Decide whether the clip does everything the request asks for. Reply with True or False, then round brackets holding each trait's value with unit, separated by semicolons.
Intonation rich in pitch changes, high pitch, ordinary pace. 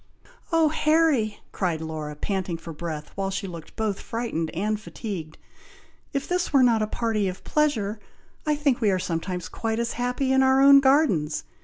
True (7.0 semitones; 215 Hz; 175 wpm)